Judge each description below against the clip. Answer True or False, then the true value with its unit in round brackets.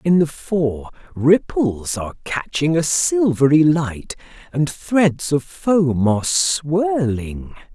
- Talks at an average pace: False (115 wpm)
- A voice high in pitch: False (150 Hz)